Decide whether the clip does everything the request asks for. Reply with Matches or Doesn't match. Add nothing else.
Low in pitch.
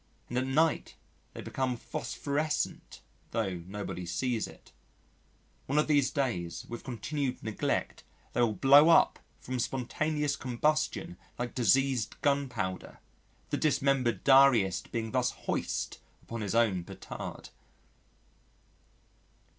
Matches